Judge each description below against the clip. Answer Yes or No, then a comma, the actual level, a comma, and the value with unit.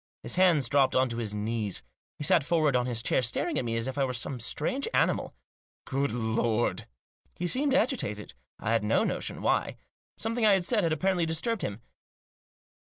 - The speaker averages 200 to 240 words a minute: Yes, fast, 205 wpm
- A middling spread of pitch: No, wide, 7.4 semitones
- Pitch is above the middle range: No, low, 130 Hz